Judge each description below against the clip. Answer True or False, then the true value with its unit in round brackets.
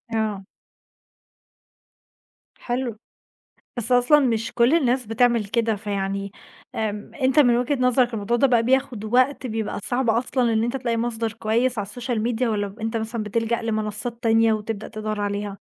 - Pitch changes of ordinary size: False (2.3 semitones)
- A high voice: True (230 Hz)